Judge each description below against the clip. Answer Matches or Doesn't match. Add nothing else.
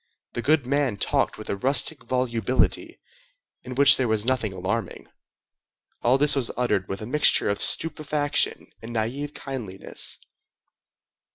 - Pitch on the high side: Doesn't match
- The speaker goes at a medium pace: Doesn't match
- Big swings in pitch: Doesn't match